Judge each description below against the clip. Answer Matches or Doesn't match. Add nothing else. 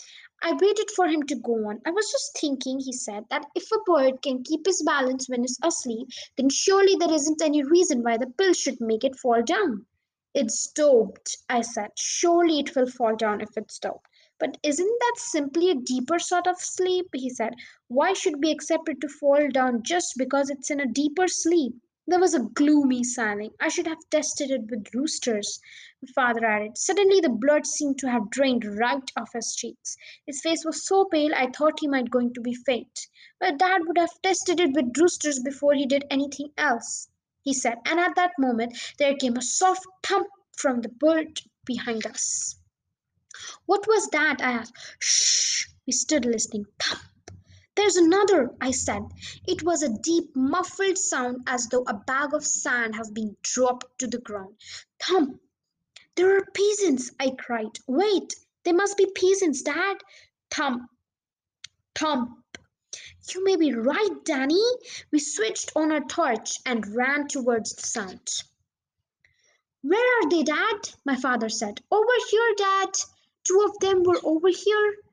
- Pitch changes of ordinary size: Doesn't match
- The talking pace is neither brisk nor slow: Matches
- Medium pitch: Doesn't match